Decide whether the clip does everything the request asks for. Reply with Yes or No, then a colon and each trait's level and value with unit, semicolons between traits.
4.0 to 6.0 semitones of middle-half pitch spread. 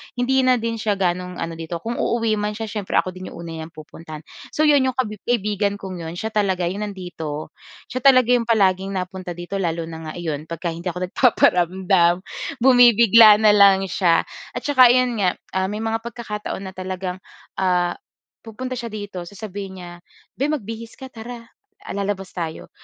Yes: average, 4.3 semitones